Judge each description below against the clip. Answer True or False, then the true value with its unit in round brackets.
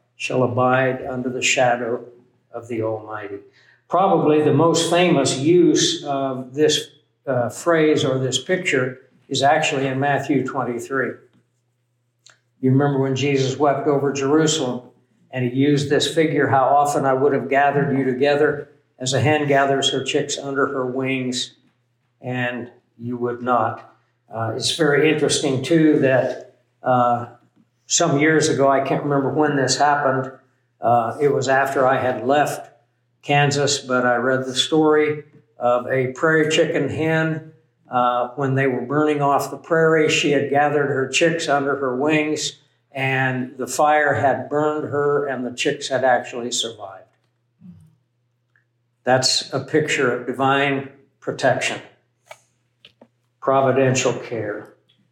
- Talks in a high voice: False (135 Hz)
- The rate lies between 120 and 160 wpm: True (140 wpm)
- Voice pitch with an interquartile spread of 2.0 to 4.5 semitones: True (2.8 semitones)